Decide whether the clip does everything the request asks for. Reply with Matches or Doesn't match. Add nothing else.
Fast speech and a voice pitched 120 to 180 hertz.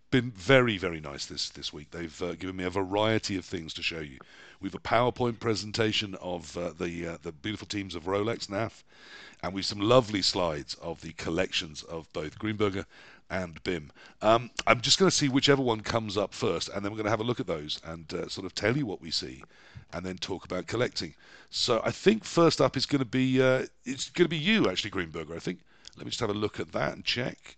Doesn't match